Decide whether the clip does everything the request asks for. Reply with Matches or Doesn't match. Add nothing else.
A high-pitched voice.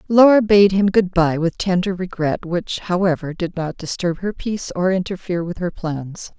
Doesn't match